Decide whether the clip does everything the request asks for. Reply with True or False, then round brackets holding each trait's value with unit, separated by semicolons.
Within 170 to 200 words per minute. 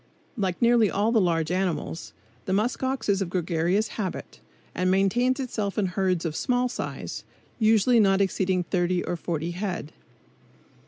False (160 wpm)